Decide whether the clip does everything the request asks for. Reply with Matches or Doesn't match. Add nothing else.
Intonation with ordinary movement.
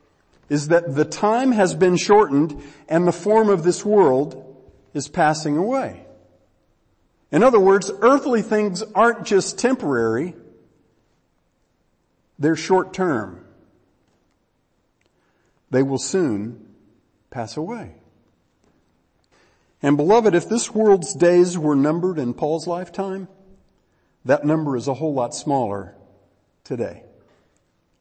Doesn't match